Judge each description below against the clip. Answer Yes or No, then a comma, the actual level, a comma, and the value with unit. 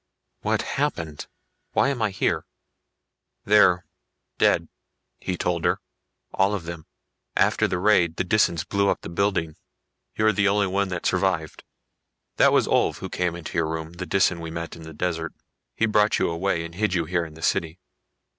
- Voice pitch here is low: Yes, very low, 90 Hz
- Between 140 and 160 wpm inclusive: No, average, 180 wpm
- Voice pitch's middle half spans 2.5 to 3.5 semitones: Yes, average, 3.1 semitones